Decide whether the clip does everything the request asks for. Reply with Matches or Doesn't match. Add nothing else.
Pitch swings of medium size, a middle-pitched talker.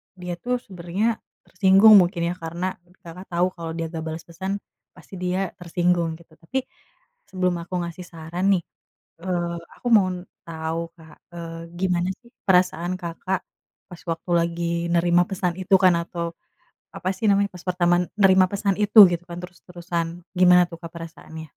Doesn't match